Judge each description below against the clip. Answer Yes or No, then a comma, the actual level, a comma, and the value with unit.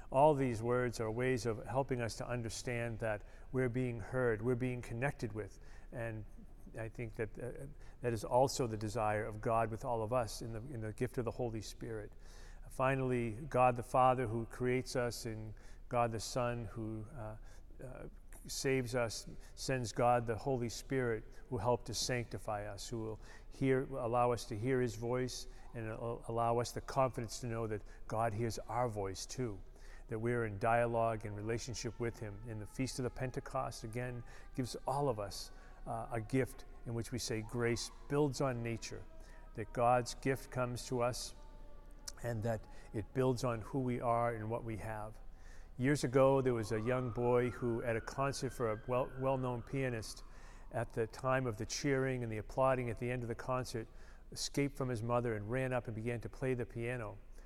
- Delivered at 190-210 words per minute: Yes, average, 195 wpm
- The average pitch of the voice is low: Yes, low, 120 Hz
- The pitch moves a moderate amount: No, narrow, 2.3 semitones